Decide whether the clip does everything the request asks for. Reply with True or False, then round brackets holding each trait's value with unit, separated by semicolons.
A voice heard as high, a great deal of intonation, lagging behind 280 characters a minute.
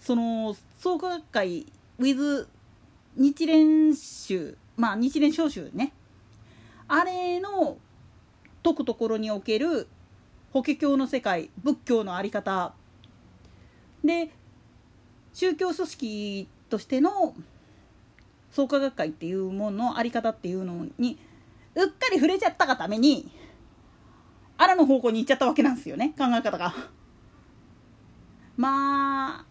True (270 Hz; 6.0 semitones; 230 characters per minute)